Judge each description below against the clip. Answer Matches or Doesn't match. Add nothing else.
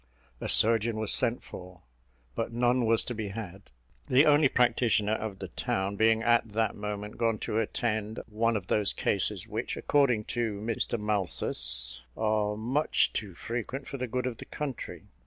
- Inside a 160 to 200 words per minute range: Matches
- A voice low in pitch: Matches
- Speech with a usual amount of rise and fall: Doesn't match